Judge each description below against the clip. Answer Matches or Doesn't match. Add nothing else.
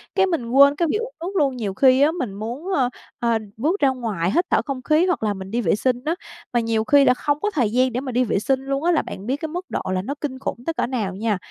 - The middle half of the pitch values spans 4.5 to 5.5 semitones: Matches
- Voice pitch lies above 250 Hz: Matches